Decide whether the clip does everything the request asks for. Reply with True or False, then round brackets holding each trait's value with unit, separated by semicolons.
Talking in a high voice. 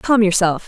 True (200 Hz)